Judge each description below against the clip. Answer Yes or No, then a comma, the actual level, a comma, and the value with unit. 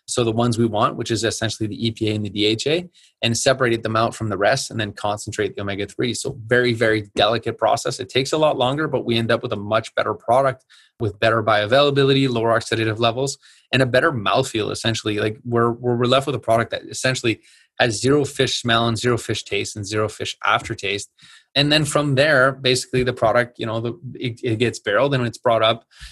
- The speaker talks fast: Yes, fast, 215 wpm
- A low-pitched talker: Yes, low, 115 Hz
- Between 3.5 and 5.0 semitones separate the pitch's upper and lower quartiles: No, narrow, 2.5 semitones